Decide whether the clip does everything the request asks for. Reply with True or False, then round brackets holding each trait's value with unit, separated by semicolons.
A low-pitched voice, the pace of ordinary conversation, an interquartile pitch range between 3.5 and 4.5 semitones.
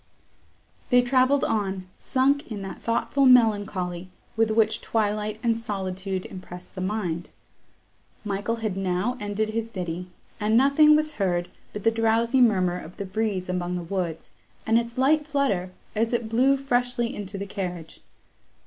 False (215 Hz; 150 wpm; 4.1 semitones)